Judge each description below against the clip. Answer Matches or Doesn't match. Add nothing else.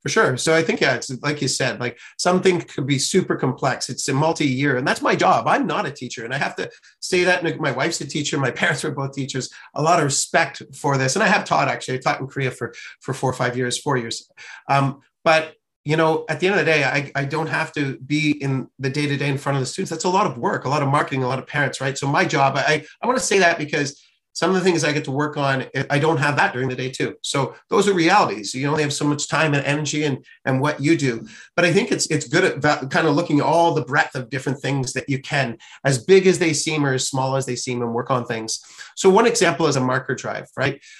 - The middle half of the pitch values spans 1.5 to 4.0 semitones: Matches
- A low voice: Doesn't match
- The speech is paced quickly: Matches